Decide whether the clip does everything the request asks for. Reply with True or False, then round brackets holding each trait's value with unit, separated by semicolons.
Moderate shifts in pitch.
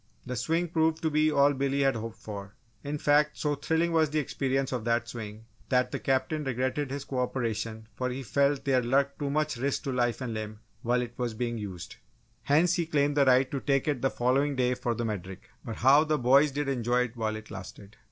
True (3.5 semitones)